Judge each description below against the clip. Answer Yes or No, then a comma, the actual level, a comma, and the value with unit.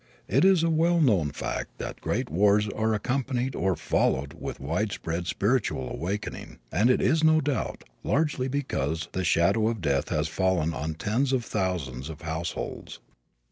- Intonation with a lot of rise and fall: Yes, wide, 8.1 semitones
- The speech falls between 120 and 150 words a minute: No, average, 160 wpm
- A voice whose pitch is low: Yes, low, 100 Hz